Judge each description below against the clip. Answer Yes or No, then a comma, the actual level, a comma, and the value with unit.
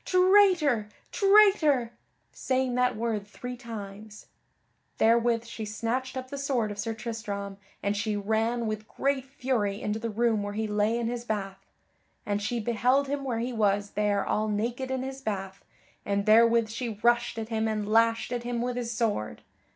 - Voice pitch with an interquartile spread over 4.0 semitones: No, average, 2.9 semitones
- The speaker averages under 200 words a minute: Yes, average, 175 wpm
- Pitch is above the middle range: Yes, high, 230 Hz